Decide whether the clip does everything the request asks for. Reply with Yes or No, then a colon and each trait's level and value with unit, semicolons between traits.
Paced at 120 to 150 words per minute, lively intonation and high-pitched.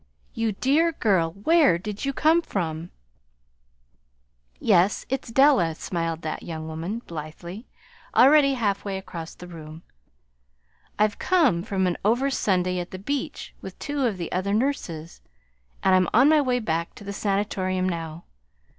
Yes: average, 145 wpm; wide, 6.9 semitones; high, 195 Hz